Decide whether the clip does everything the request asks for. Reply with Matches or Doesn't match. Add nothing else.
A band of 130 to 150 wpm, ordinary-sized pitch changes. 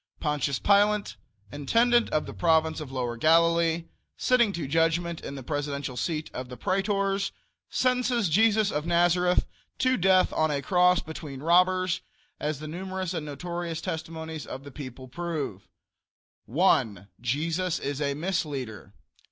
Matches